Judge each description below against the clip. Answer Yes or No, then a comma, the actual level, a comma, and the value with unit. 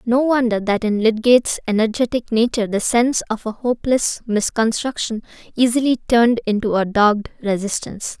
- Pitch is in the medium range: No, high, 230 Hz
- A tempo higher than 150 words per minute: No, average, 140 wpm